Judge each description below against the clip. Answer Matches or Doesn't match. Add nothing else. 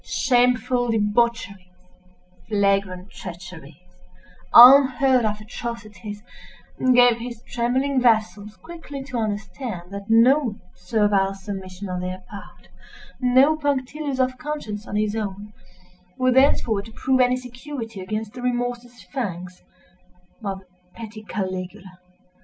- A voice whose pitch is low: Doesn't match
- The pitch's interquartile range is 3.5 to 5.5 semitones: Matches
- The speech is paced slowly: Matches